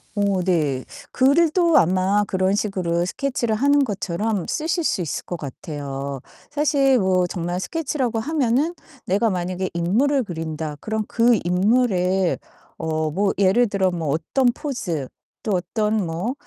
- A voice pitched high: Yes, high, 195 Hz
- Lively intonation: Yes, wide, 6.0 semitones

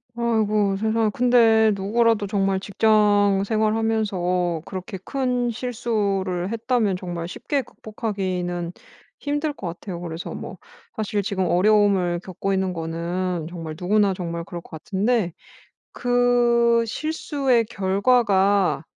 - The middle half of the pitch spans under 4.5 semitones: Yes, average, 4.0 semitones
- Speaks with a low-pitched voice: No, high, 205 Hz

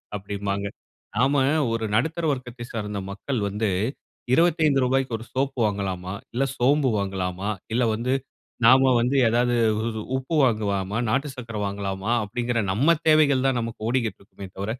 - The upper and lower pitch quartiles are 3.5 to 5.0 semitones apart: Yes, average, 4.6 semitones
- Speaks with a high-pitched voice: No, low, 115 Hz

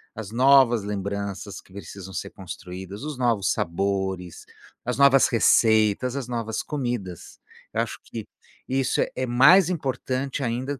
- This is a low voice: Yes, low, 115 Hz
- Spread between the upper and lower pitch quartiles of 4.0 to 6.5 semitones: Yes, average, 4.7 semitones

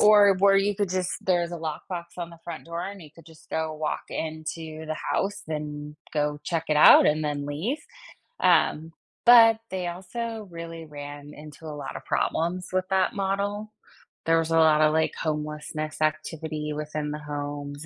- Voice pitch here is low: No, medium, 160 Hz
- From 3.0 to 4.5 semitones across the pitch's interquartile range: Yes, average, 3.3 semitones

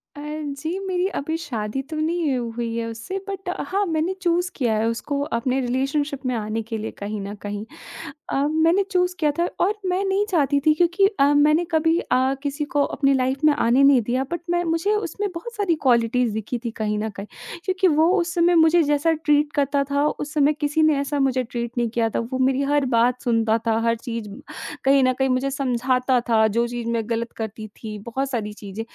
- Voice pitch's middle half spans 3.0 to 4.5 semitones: No, wide, 5.4 semitones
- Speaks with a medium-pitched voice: No, very high, 275 Hz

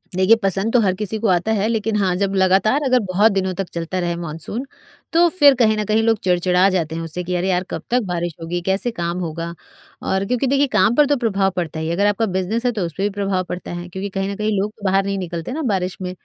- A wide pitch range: No, average, 3.5 semitones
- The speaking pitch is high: Yes, high, 195 Hz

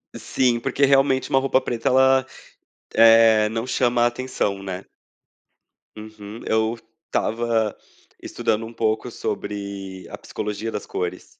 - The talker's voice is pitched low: Yes, low, 115 Hz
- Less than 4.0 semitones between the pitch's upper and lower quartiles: Yes, average, 2.7 semitones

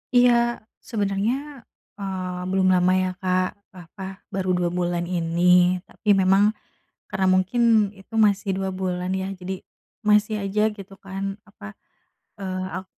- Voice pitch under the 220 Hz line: Yes, high, 190 Hz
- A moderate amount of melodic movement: No, narrow, 1.8 semitones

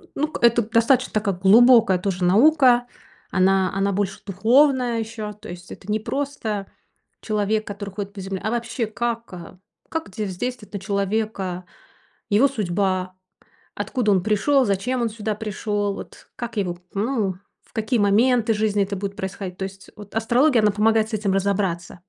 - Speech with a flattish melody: No, average, 3.0 semitones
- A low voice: No, high, 210 Hz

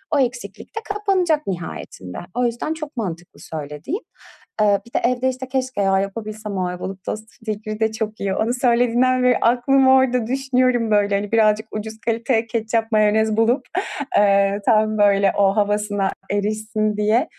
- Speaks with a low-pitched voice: No, high, 220 Hz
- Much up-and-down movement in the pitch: No, average, 3.4 semitones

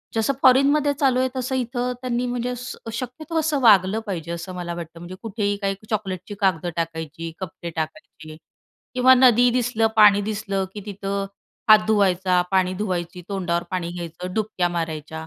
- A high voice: Yes, high, 200 Hz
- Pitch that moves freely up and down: Yes, wide, 5.9 semitones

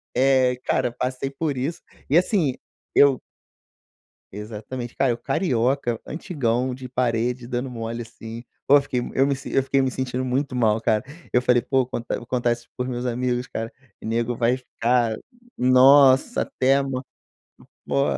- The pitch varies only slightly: Yes, narrow, 2.1 semitones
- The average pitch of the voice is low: Yes, low, 125 Hz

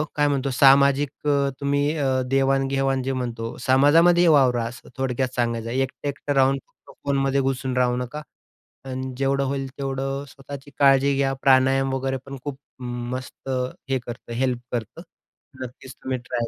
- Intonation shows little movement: Yes, narrow, 1.3 semitones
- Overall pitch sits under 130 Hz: No, low, 135 Hz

